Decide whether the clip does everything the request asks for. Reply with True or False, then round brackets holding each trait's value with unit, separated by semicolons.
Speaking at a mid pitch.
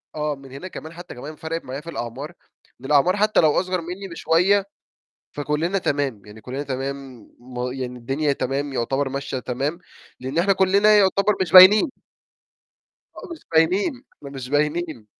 True (150 Hz)